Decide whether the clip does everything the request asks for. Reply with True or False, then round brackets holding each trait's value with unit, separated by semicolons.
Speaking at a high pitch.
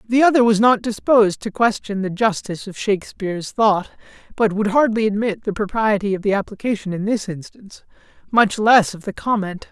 True (210 Hz)